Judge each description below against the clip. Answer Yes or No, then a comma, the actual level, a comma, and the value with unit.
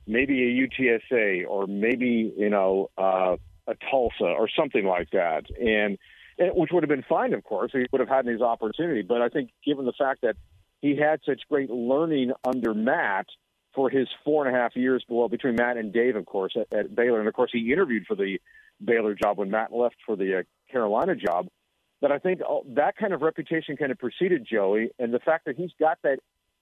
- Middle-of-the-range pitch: No, low, 125 Hz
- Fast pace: Yes, fast, 220 wpm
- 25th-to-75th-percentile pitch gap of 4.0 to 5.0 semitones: Yes, average, 4.7 semitones